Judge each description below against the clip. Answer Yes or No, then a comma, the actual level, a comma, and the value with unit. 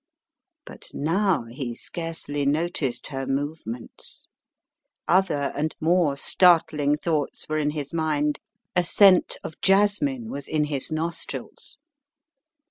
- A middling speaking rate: No, slow, 115 wpm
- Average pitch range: Yes, average, 3.4 semitones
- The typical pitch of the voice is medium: Yes, medium, 155 Hz